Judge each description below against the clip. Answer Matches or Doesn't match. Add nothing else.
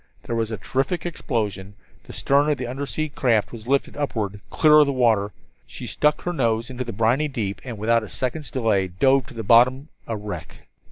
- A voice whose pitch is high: Doesn't match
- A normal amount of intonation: Matches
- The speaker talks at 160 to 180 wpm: Doesn't match